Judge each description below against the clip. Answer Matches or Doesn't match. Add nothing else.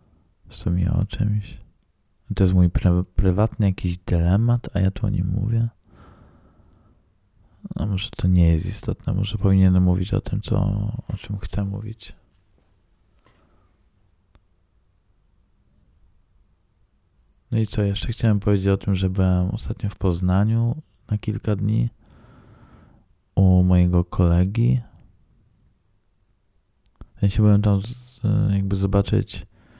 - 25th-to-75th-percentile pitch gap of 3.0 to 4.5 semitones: Doesn't match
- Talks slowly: Doesn't match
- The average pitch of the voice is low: Matches